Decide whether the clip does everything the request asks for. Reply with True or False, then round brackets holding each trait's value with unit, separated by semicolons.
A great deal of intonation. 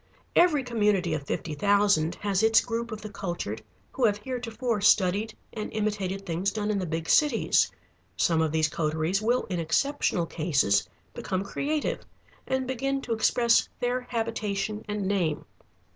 False (5.0 semitones)